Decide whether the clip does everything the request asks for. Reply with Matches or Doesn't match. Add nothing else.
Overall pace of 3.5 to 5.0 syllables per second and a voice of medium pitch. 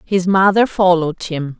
Matches